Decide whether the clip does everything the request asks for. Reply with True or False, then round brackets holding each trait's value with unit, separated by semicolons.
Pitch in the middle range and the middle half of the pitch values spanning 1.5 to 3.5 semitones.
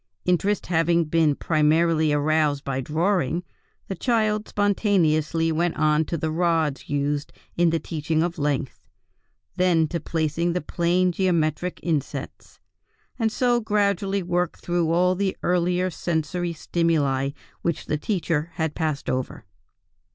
True (165 Hz; 2.7 semitones)